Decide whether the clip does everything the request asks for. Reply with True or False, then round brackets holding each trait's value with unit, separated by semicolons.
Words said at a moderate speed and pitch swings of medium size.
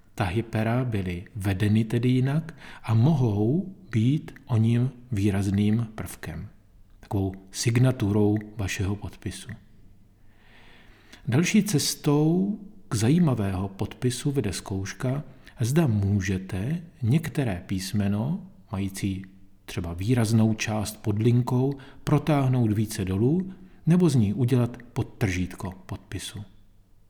False (95 wpm; 4.6 semitones)